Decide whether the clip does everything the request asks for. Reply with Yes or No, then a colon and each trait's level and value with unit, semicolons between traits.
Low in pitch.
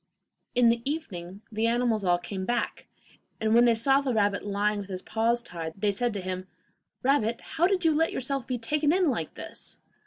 No: high, 230 Hz